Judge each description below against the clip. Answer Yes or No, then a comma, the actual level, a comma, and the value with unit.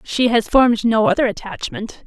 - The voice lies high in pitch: Yes, high, 230 Hz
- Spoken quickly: No, average, 175 wpm